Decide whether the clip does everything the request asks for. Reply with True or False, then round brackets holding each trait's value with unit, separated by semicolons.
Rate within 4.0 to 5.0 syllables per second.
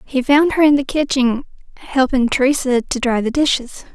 True (4.9 syllables/s)